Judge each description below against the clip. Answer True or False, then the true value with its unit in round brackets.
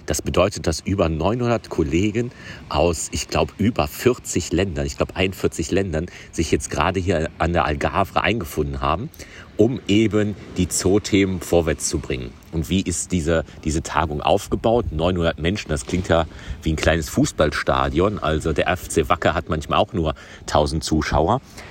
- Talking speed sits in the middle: True (160 wpm)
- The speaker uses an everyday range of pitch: True (3.7 semitones)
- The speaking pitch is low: True (85 Hz)